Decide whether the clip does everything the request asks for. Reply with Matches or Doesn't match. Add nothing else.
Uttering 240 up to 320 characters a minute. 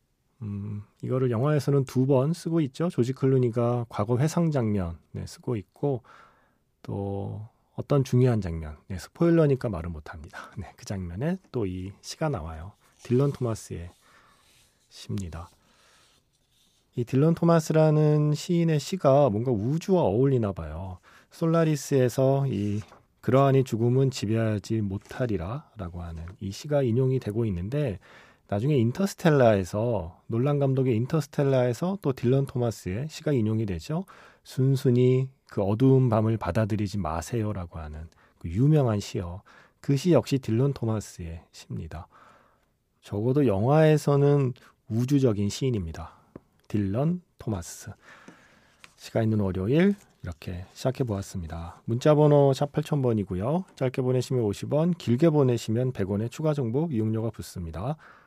Matches